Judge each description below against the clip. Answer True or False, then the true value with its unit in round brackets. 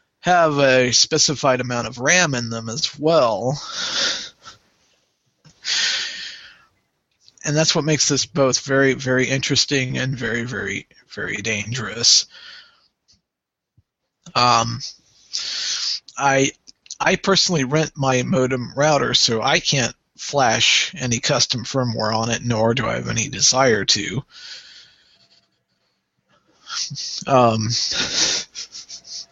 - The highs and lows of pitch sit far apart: False (3.4 semitones)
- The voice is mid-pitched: False (130 Hz)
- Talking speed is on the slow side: True (100 wpm)